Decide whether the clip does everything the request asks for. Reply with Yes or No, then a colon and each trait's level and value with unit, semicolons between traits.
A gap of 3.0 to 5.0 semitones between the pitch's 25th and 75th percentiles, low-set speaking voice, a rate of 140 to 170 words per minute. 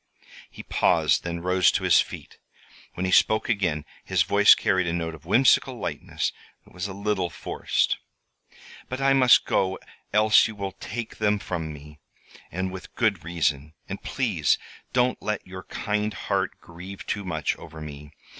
Yes: average, 4.1 semitones; very low, 95 Hz; average, 165 wpm